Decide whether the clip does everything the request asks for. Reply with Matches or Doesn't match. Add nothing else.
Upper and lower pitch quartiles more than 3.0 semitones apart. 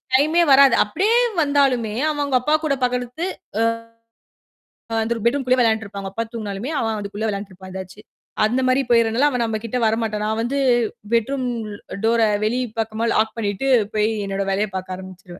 Matches